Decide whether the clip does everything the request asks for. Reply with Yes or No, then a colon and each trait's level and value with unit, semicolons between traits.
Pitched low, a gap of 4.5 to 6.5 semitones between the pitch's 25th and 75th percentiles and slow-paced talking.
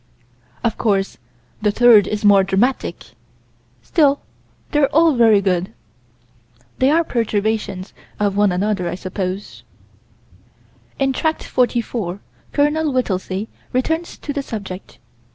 No: high, 215 Hz; wide, 5.6 semitones; slow, 115 wpm